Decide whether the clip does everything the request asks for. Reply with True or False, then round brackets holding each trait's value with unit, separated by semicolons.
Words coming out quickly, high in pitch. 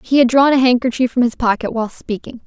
True (245 wpm; 245 Hz)